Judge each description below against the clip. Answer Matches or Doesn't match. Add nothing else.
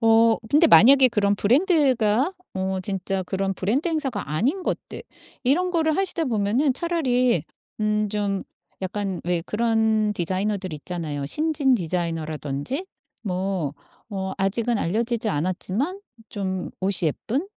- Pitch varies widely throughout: Matches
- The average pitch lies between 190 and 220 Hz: Matches